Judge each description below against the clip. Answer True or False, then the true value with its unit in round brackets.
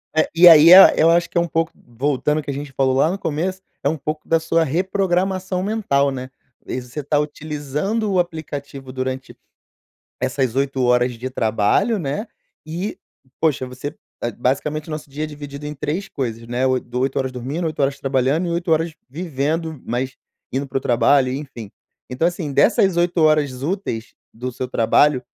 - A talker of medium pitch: True (145 Hz)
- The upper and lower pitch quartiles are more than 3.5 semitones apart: True (4.1 semitones)